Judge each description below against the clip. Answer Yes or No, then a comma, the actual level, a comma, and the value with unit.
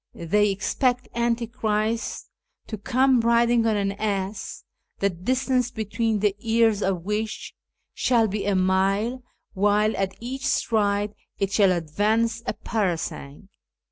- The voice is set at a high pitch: Yes, high, 215 Hz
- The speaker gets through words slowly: Yes, slow, 125 wpm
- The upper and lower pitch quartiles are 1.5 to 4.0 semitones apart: Yes, average, 2.8 semitones